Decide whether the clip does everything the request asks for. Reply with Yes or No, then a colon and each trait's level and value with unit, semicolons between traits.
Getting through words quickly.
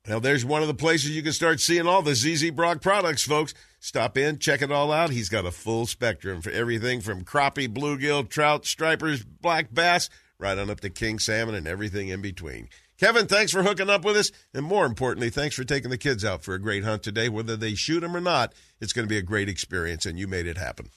Yes: fast, 245 wpm